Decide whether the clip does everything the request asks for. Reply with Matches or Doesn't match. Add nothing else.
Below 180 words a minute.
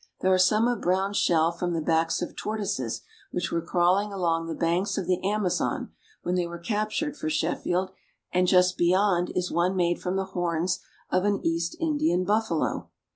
Doesn't match